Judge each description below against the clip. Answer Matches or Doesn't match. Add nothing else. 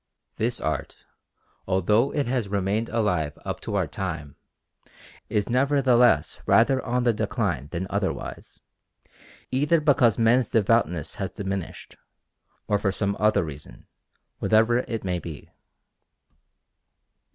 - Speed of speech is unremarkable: Doesn't match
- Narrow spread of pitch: Doesn't match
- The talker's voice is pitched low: Matches